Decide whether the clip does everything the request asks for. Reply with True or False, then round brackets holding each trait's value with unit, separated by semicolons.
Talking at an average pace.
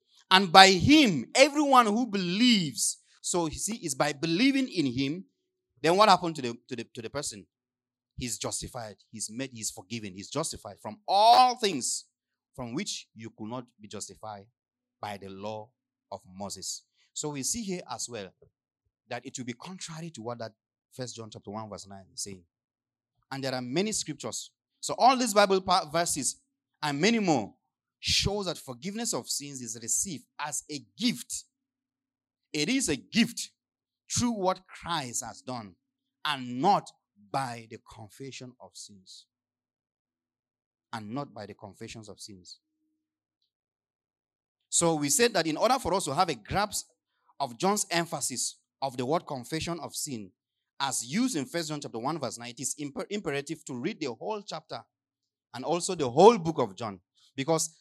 True (165 wpm)